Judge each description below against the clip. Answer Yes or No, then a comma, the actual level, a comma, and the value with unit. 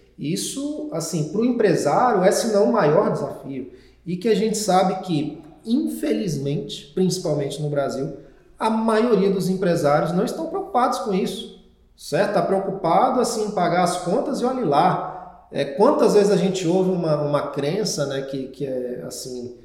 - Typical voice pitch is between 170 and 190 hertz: Yes, medium, 185 Hz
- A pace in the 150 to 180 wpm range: Yes, average, 165 wpm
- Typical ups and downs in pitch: No, wide, 6.6 semitones